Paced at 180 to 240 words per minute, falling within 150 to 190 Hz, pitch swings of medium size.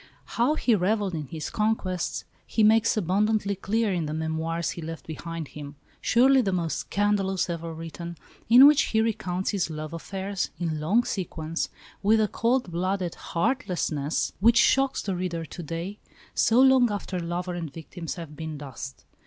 No: average, 165 wpm; medium, 185 Hz; average, 4.7 semitones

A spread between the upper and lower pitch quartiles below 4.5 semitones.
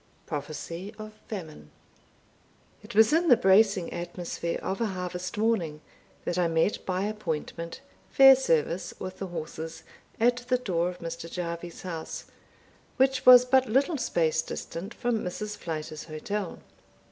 No: average, 4.9 semitones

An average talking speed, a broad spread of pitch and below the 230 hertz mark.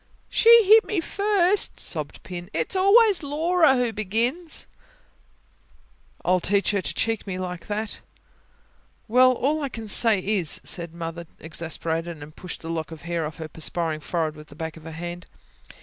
Yes: average, 165 wpm; wide, 9.0 semitones; medium, 185 Hz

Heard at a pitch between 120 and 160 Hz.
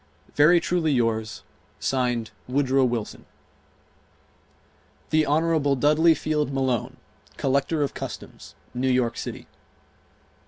Yes: low, 135 Hz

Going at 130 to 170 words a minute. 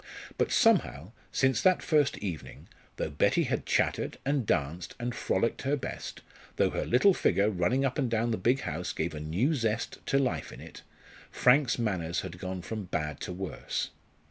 No: average, 180 wpm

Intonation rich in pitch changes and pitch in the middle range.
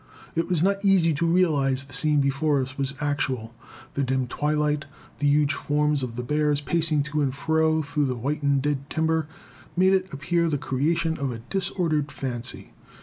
No: narrow, 2.6 semitones; medium, 150 Hz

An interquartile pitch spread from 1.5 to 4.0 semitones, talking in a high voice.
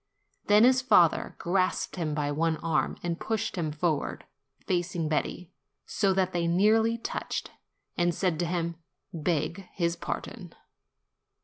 No: average, 2.8 semitones; medium, 175 Hz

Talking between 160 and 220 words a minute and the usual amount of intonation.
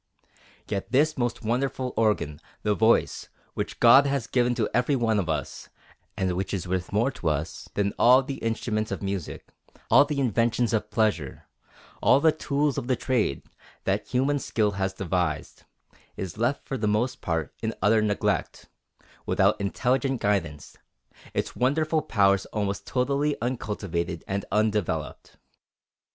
No: average, 145 wpm; average, 4.6 semitones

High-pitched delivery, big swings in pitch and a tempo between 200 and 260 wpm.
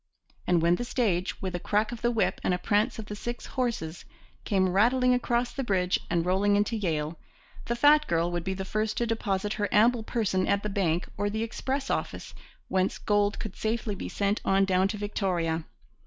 No: high, 205 Hz; average, 3.7 semitones; fast, 205 wpm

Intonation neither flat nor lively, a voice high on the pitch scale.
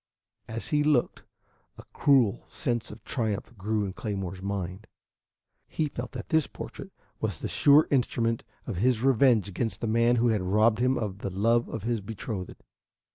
No: average, 3.4 semitones; low, 115 Hz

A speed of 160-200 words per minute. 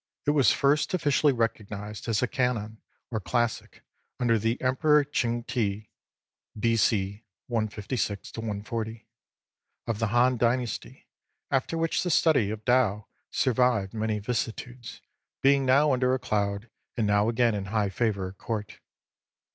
No: average, 145 wpm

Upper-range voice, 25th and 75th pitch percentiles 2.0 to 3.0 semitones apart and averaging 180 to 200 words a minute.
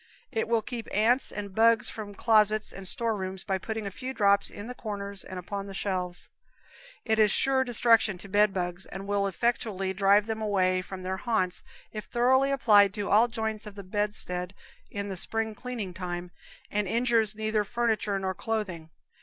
Yes: high, 205 Hz; narrow, 2.6 semitones; average, 185 wpm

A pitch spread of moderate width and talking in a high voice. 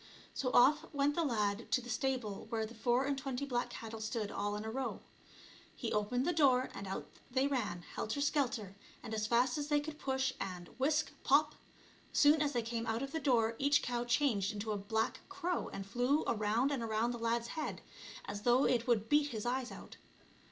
Yes: average, 4.1 semitones; high, 245 Hz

